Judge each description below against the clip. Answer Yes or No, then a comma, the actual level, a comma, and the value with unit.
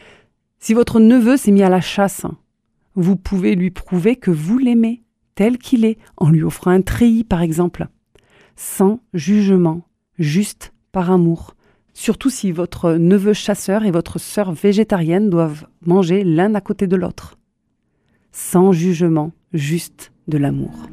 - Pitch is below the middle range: No, high, 190 Hz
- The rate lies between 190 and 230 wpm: No, slow, 145 wpm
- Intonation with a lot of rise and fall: No, average, 3.5 semitones